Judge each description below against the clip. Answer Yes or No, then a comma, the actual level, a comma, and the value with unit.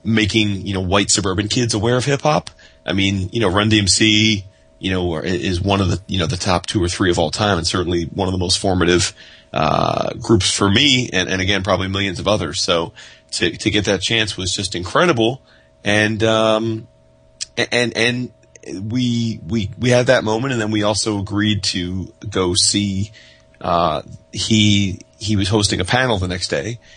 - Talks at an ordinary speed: Yes, average, 195 wpm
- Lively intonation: No, average, 3.2 semitones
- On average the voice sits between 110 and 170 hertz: No, low, 100 Hz